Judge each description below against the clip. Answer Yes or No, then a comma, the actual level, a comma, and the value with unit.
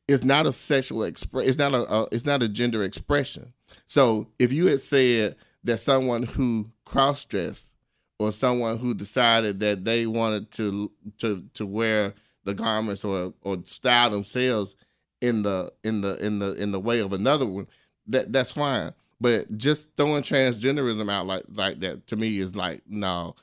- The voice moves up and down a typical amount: Yes, average, 3.9 semitones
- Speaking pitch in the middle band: No, low, 115 Hz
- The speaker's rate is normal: Yes, average, 175 wpm